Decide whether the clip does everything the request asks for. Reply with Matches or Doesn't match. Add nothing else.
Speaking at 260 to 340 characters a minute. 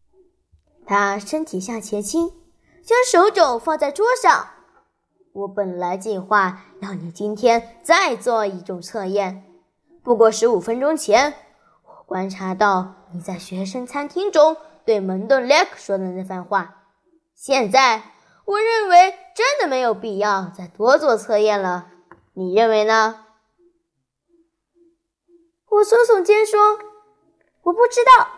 Doesn't match